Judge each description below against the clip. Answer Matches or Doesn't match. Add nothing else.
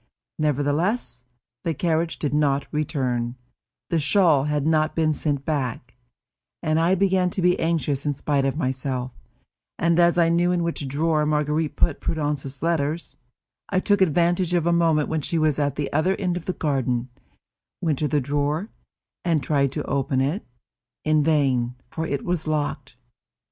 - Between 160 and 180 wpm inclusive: Matches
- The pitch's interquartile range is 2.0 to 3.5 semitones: Matches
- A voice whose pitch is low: Doesn't match